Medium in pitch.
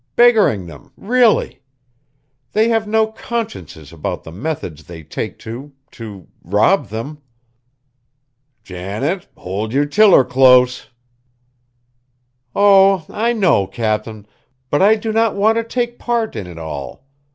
Yes: medium, 145 Hz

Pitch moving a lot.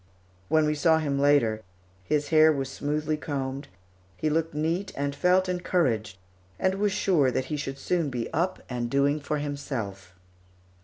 No: average, 3.0 semitones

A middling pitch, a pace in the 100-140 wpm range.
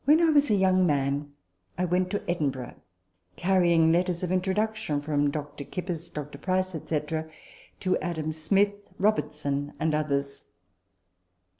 Yes: medium, 170 Hz; slow, 135 wpm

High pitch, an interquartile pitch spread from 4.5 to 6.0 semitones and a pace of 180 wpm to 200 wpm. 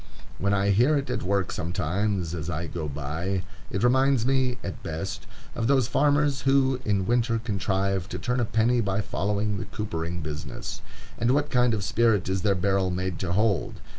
No: low, 100 Hz; average, 4.9 semitones; average, 185 wpm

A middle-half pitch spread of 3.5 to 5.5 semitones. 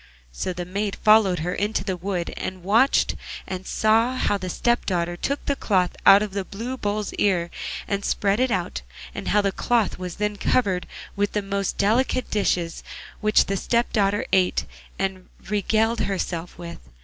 No: average, 2.7 semitones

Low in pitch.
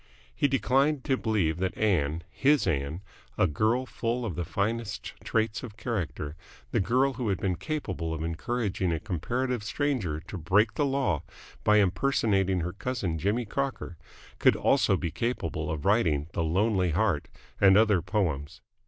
Yes: low, 100 Hz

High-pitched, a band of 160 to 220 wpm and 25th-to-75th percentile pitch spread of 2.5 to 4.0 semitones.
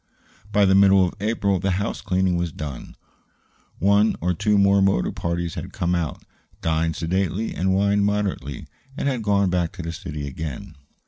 No: very low, 95 Hz; average, 170 wpm; average, 3.2 semitones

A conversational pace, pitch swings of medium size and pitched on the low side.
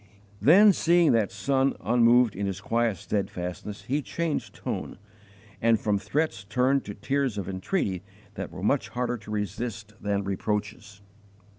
Yes: average, 145 wpm; average, 4.7 semitones; low, 110 Hz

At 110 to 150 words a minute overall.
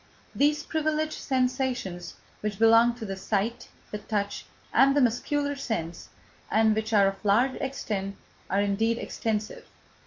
Yes: slow, 135 wpm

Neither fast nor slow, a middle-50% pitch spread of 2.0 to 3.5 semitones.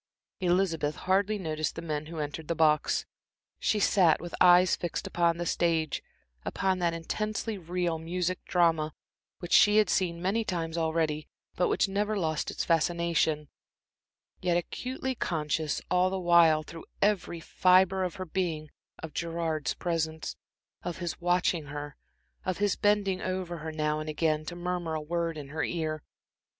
Yes: average, 160 wpm; narrow, 2.5 semitones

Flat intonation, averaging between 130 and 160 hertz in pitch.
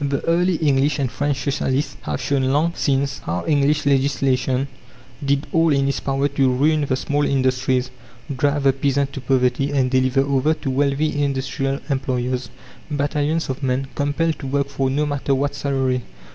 Yes: narrow, 1.5 semitones; medium, 140 Hz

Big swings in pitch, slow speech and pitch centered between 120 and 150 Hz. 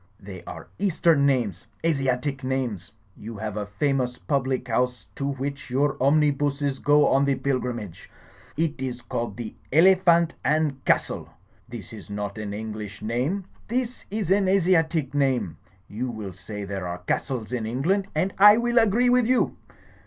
No: wide, 6.5 semitones; average, 155 wpm; low, 135 Hz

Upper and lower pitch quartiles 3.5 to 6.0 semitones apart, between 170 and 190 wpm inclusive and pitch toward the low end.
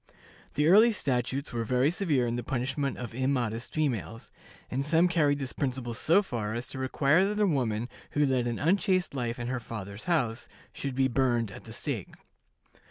Yes: average, 3.9 semitones; average, 185 wpm; low, 130 Hz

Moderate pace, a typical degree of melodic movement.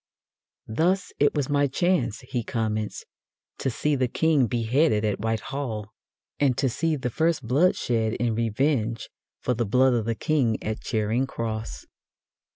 Yes: average, 160 wpm; average, 4.4 semitones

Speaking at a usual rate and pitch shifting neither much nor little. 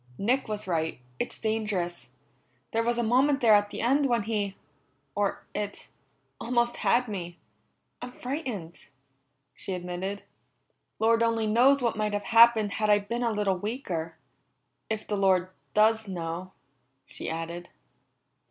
Yes: average, 145 wpm; average, 3.8 semitones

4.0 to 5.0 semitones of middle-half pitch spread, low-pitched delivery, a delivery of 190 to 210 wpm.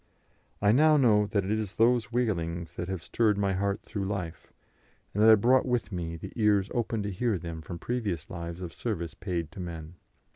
Yes: average, 4.5 semitones; low, 100 Hz; fast, 205 wpm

